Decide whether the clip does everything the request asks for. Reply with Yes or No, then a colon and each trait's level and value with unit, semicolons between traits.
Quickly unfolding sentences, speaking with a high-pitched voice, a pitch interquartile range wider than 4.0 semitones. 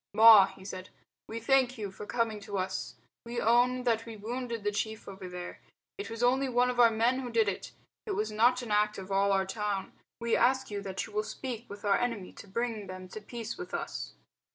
No: fast, 225 wpm; high, 220 Hz; average, 3.2 semitones